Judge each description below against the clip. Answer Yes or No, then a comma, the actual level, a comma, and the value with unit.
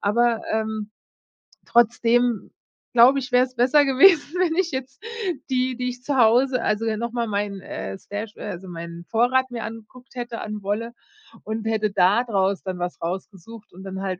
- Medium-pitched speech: No, high, 230 Hz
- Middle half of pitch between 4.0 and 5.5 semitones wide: No, average, 3.6 semitones